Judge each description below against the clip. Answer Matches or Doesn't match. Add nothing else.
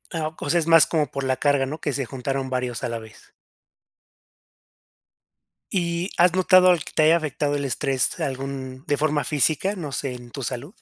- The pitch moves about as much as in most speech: Matches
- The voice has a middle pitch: Matches